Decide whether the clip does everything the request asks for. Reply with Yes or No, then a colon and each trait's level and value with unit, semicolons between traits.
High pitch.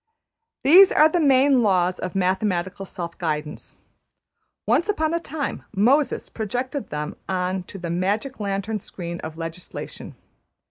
Yes: high, 195 Hz